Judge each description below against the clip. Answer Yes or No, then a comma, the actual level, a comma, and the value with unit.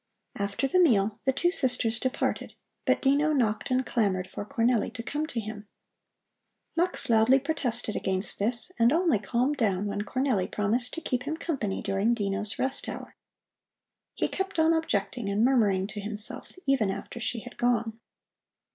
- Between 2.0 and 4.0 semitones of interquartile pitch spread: No, average, 4.6 semitones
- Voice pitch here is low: No, high, 235 Hz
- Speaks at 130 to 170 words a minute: Yes, average, 165 wpm